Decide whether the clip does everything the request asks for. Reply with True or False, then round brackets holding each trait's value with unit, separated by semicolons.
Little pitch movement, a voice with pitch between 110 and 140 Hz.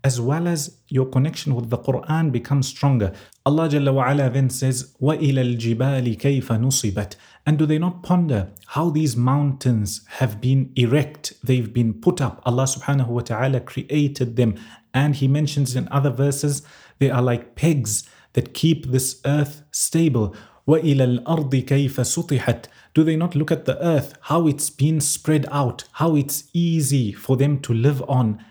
False (3.1 semitones; 135 Hz)